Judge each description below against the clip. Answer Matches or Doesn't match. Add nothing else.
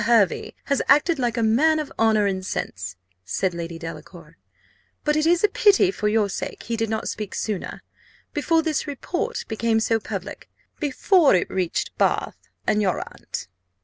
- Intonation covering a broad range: Matches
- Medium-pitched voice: Doesn't match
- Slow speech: Doesn't match